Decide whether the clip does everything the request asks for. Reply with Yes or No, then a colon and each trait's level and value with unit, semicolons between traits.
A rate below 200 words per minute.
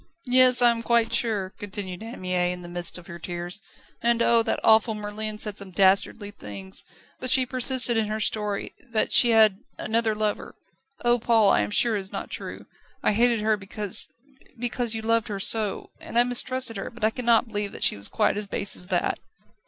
No: fast, 205 wpm